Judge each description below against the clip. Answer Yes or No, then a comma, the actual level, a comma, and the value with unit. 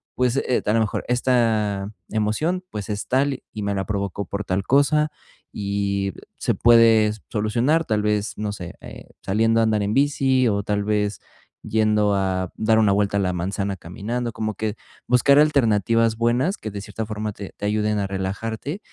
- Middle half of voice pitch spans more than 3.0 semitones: No, narrow, 2.6 semitones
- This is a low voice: Yes, low, 105 Hz